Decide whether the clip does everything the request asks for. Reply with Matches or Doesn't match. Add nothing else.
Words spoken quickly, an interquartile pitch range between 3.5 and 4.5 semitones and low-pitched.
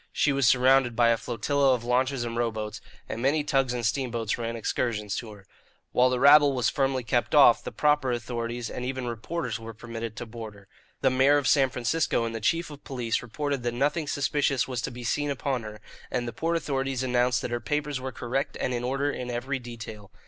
Doesn't match